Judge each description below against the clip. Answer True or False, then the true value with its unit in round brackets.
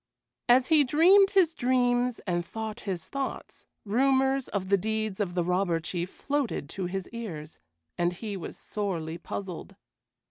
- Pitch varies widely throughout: True (6.4 semitones)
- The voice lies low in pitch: False (215 Hz)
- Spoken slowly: False (150 wpm)